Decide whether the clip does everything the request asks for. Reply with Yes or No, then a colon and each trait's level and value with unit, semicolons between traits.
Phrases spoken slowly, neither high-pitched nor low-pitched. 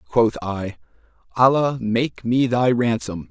No: slow, 125 wpm; low, 120 Hz